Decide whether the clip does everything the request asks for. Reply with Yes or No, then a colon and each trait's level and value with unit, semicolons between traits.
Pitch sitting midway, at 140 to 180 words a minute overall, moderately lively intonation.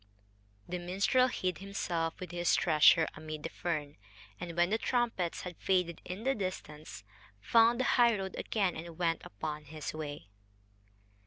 Yes: medium, 175 Hz; average, 150 wpm; average, 3.8 semitones